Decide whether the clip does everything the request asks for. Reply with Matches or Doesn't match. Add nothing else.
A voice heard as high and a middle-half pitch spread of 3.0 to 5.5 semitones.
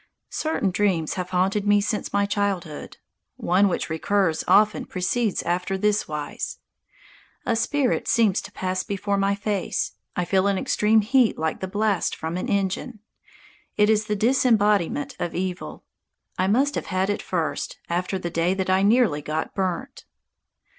Doesn't match